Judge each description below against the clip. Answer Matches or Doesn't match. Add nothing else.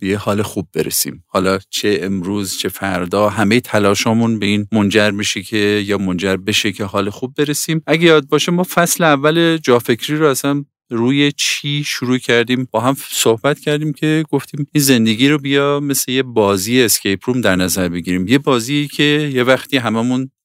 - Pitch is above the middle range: Doesn't match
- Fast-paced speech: Matches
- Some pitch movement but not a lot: Doesn't match